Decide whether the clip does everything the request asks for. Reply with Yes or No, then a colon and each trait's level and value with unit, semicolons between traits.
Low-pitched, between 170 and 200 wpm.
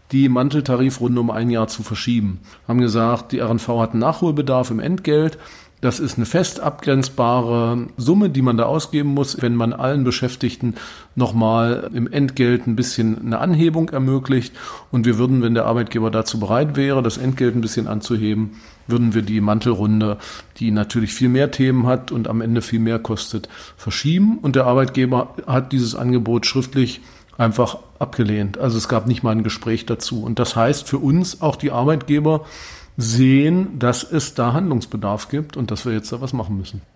Yes: low, 120 Hz; average, 175 wpm